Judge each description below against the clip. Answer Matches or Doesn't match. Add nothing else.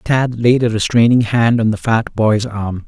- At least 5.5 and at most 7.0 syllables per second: Doesn't match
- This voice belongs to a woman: Doesn't match